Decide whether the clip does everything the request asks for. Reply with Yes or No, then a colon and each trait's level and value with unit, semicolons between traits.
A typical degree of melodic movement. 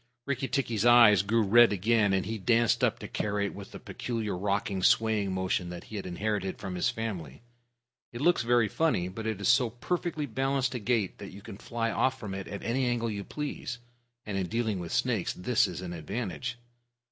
Yes: average, 3.7 semitones